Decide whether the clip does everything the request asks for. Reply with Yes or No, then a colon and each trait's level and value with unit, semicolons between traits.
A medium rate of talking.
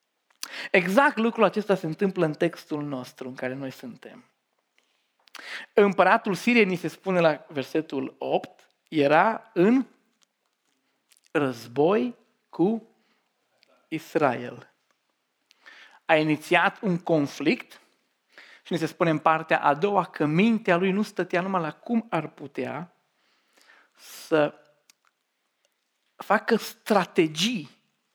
No: slow, 105 wpm